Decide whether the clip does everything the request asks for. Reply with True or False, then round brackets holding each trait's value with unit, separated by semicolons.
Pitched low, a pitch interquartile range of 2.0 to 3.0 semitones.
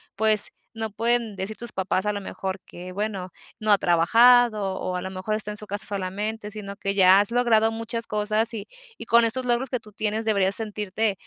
False (210 Hz; 2.4 semitones)